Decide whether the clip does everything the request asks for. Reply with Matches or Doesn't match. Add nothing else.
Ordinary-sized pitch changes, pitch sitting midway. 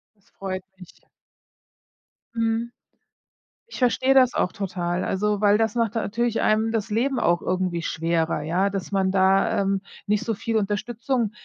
Doesn't match